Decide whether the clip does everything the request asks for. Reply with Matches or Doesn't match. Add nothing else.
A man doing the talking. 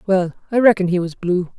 Doesn't match